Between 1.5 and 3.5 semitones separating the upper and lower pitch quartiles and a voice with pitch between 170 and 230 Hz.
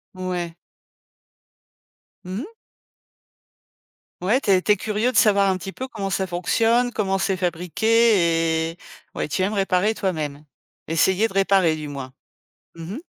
No: average, 3.9 semitones; high, 190 Hz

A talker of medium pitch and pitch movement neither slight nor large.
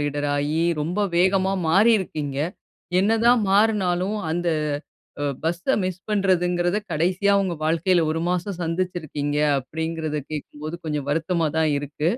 Yes: medium, 175 Hz; average, 3.5 semitones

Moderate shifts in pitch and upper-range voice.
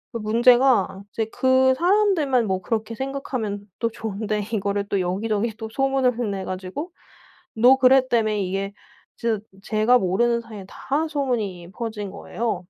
Yes: average, 4.3 semitones; high, 225 Hz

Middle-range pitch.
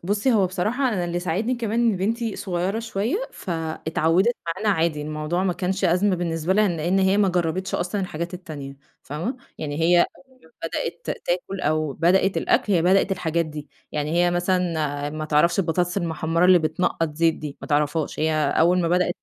Yes: medium, 175 Hz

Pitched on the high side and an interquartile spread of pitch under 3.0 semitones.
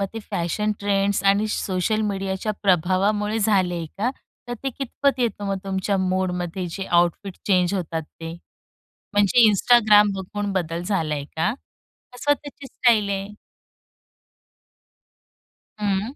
Yes: high, 195 Hz; narrow, 2.6 semitones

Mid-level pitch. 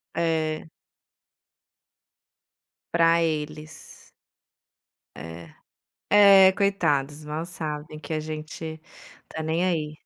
Yes: medium, 160 Hz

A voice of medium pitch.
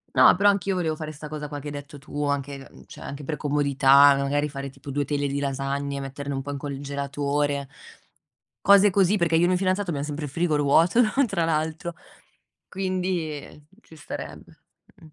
Yes: medium, 145 Hz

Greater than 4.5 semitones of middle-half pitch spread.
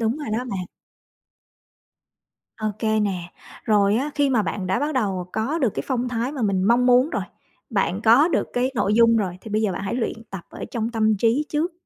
No: average, 3.9 semitones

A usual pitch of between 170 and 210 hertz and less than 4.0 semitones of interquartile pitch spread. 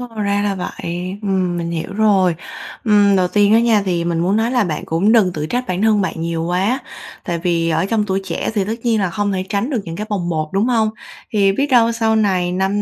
Yes: high, 195 Hz; average, 3.4 semitones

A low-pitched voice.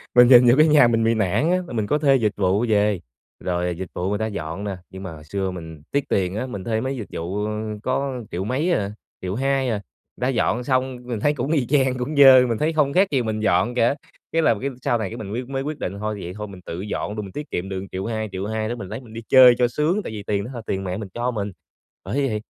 Yes: low, 110 Hz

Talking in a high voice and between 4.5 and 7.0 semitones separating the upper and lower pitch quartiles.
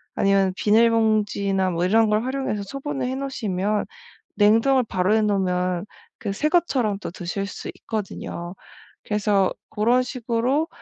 No: high, 210 Hz; average, 4.1 semitones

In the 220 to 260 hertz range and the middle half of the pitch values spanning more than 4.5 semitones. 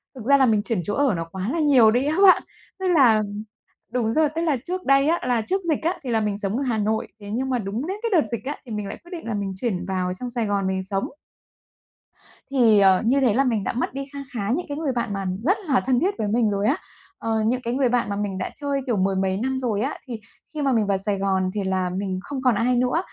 Yes: high, 235 Hz; average, 5.2 semitones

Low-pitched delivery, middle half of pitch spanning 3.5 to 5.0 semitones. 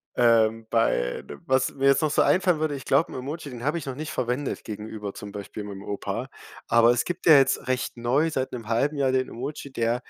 Yes: low, 130 Hz; average, 3.9 semitones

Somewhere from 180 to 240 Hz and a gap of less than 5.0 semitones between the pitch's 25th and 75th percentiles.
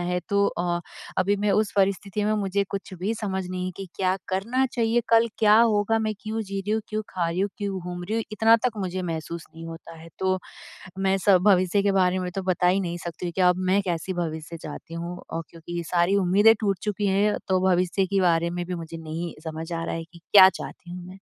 Yes: medium, 185 Hz; average, 2.7 semitones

